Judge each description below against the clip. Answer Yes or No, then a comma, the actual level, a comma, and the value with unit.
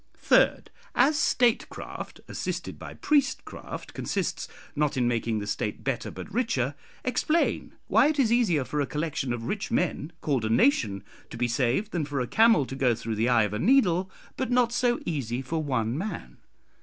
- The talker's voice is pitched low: No, medium, 150 Hz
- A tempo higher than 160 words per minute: Yes, average, 180 wpm